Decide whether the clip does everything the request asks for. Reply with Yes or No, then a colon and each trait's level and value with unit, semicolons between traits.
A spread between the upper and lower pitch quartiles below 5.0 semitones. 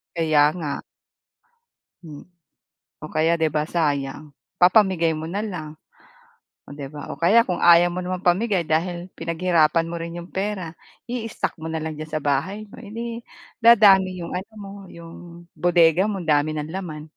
Yes: average, 3.3 semitones